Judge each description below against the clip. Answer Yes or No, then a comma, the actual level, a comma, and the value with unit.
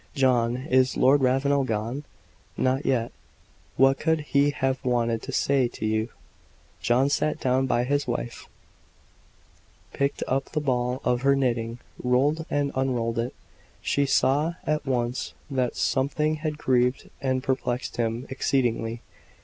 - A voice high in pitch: No, low, 130 Hz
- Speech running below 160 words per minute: Yes, average, 140 wpm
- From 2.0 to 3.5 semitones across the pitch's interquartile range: Yes, narrow, 2.4 semitones